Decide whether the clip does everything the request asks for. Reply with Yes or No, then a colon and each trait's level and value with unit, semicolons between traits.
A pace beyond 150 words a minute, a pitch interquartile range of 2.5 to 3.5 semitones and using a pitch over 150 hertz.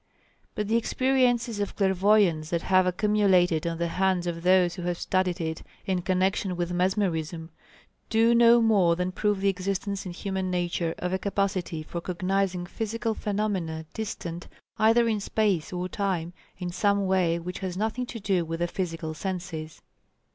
Yes: average, 165 wpm; average, 2.8 semitones; medium, 185 Hz